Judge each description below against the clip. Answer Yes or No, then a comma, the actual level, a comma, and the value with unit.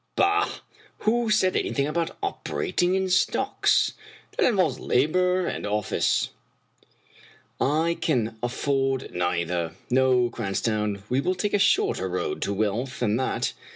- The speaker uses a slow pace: Yes, slow, 130 wpm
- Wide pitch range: Yes, wide, 8.5 semitones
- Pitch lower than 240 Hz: Yes, low, 135 Hz